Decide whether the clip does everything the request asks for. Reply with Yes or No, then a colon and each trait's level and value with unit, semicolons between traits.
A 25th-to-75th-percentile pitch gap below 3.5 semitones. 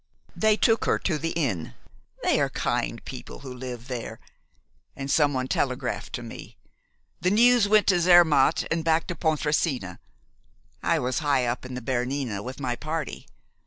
No: average, 4.7 semitones